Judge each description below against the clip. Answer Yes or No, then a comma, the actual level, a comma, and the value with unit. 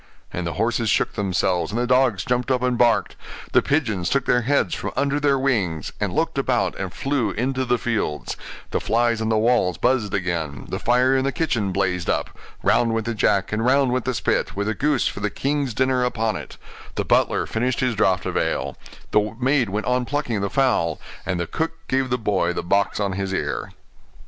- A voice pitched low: Yes, low, 115 Hz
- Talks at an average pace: No, fast, 215 wpm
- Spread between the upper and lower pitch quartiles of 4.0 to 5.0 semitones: Yes, average, 4.6 semitones